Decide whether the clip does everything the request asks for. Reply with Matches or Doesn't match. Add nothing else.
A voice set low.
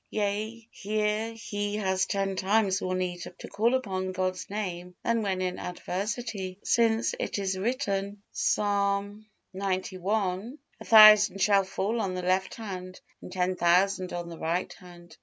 Doesn't match